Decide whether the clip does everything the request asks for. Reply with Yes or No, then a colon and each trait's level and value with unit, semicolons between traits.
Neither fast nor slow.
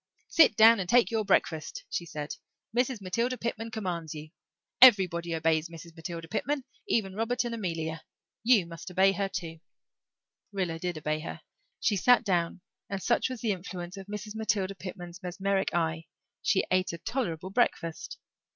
Yes: average, 160 wpm